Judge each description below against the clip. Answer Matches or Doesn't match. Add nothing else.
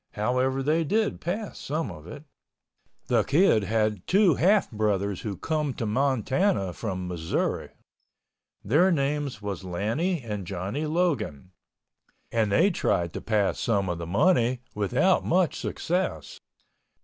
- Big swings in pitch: Matches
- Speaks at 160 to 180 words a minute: Doesn't match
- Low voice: Matches